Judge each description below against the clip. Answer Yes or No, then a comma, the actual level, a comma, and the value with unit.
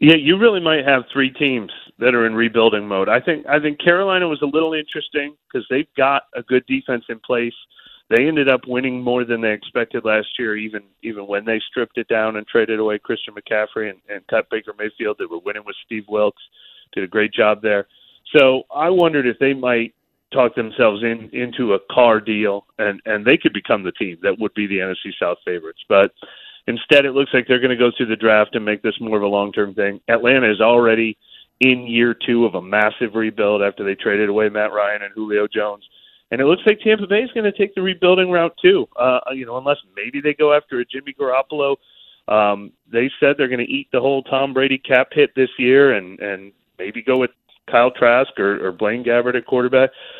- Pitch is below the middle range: Yes, low, 125 Hz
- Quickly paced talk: Yes, fast, 220 wpm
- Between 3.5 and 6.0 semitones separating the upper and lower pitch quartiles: Yes, average, 4.7 semitones